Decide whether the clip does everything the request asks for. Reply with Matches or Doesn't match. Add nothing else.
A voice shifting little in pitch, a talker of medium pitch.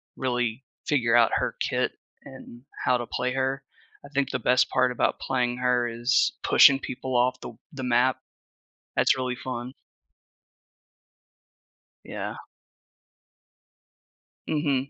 Doesn't match